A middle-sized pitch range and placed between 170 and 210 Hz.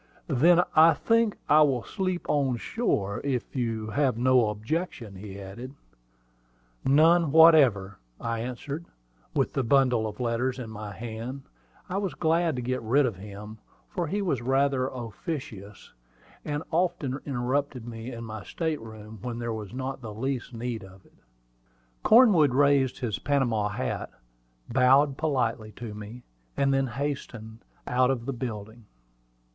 No: average, 4.4 semitones; low, 125 Hz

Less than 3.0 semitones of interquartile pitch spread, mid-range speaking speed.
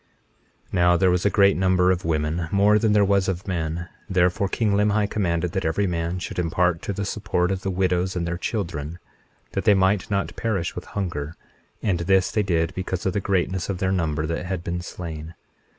No: narrow, 2.5 semitones; fast, 210 wpm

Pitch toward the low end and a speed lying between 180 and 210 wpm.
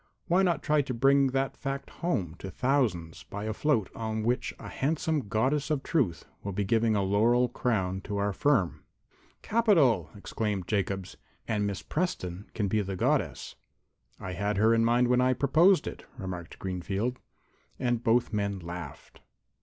No: low, 110 Hz; average, 165 wpm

